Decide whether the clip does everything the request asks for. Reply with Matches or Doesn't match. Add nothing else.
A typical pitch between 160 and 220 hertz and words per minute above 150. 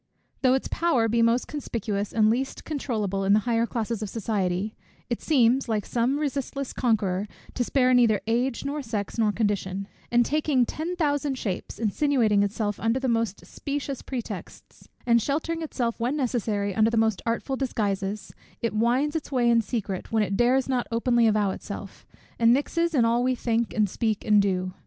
Doesn't match